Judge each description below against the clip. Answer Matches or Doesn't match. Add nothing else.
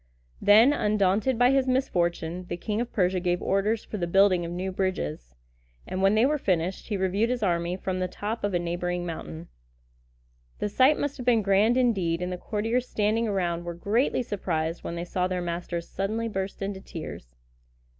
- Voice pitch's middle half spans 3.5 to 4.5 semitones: Matches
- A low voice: Doesn't match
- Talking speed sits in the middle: Matches